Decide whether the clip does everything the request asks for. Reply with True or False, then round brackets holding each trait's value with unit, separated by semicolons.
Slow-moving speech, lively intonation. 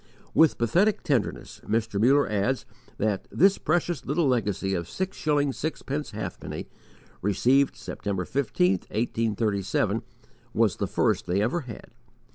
True (125 wpm; 6.0 semitones)